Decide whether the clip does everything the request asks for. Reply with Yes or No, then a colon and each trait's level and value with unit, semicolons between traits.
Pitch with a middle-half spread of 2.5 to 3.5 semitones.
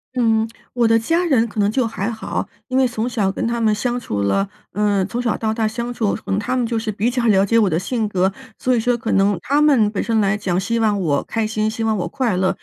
Yes: average, 2.8 semitones